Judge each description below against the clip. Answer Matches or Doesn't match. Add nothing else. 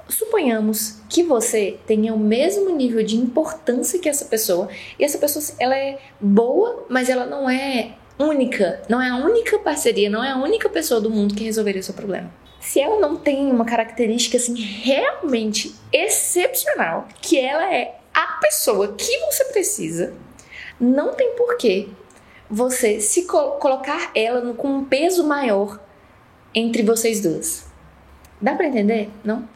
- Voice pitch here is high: Matches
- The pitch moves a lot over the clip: Matches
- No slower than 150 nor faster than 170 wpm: Matches